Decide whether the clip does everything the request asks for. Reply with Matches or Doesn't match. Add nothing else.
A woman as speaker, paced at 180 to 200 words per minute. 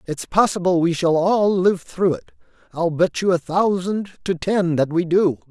Doesn't match